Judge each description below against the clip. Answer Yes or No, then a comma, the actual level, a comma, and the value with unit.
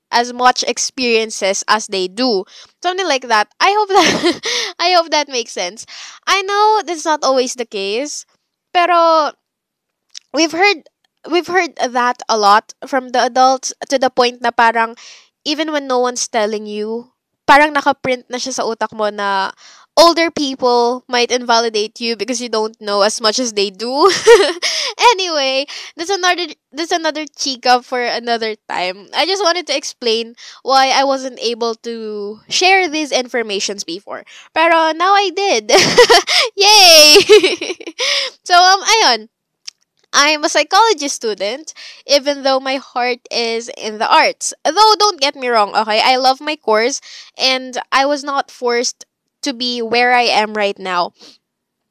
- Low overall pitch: No, very high, 260 Hz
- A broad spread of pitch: Yes, wide, 6.2 semitones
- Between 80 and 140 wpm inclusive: No, fast, 155 wpm